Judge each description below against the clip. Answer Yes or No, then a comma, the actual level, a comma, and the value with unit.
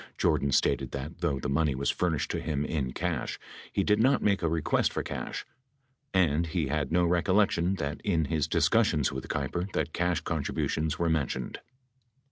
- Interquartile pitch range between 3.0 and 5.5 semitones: Yes, average, 3.4 semitones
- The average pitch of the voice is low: Yes, very low, 80 Hz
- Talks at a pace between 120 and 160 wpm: No, average, 175 wpm